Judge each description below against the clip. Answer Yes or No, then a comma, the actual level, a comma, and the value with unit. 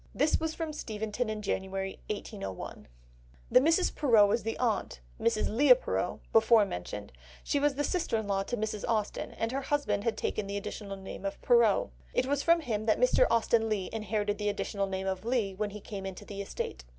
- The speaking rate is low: No, average, 200 wpm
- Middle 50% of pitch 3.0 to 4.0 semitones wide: Yes, average, 3.6 semitones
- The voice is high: Yes, high, 215 Hz